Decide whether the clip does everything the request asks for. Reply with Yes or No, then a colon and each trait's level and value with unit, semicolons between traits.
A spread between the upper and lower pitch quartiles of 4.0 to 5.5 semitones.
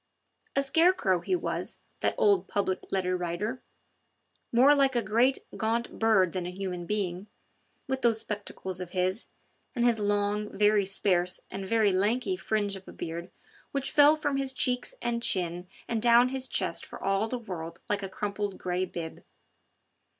Yes: average, 4.3 semitones